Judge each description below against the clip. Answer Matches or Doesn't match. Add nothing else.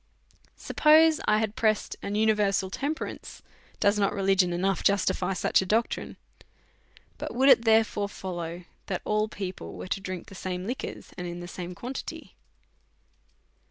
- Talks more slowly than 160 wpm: Matches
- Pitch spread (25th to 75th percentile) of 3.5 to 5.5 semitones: Doesn't match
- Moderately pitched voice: Doesn't match